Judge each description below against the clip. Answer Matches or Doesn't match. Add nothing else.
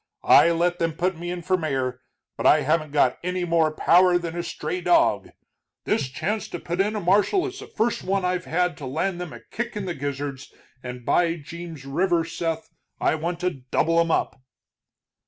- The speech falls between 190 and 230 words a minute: Matches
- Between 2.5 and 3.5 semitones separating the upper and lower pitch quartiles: Matches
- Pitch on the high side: Doesn't match